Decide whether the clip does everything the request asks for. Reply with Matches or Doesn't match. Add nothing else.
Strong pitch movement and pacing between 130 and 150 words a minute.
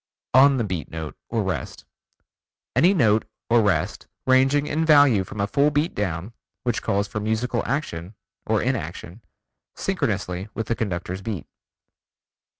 Matches